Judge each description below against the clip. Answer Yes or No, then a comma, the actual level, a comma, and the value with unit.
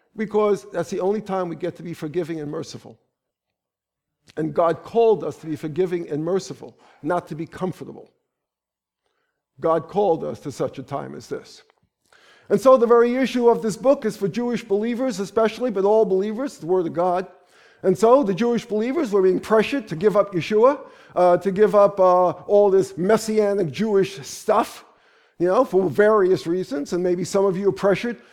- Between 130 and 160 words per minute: No, average, 185 wpm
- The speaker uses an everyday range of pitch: Yes, average, 4.0 semitones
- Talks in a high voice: Yes, high, 195 Hz